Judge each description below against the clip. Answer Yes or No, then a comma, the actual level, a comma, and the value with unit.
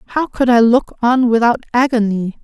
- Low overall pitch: No, high, 235 Hz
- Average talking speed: Yes, average, 170 wpm